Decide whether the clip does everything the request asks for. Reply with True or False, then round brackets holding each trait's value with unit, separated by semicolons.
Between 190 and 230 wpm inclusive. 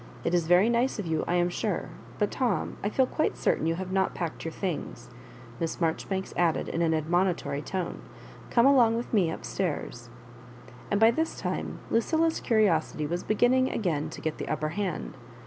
True (200 wpm)